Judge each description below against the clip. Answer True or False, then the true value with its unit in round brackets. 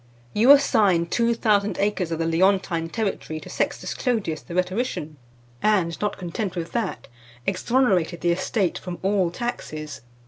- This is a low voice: False (190 Hz)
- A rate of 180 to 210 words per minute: False (145 wpm)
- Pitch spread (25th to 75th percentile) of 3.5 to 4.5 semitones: True (4.2 semitones)